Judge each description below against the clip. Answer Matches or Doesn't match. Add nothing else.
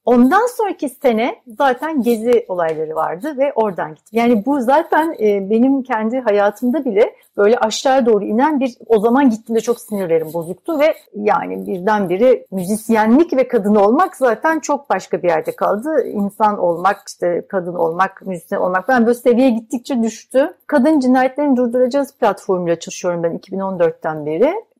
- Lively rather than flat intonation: Matches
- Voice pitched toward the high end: Matches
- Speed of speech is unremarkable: Doesn't match